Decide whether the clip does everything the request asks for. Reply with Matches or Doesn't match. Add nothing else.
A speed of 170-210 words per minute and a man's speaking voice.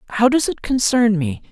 Matches